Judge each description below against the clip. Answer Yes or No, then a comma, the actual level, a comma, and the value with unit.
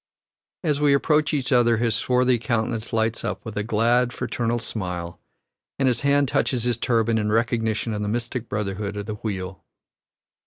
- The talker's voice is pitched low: Yes, low, 115 Hz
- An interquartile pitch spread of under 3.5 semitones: Yes, average, 2.7 semitones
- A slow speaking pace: No, average, 170 wpm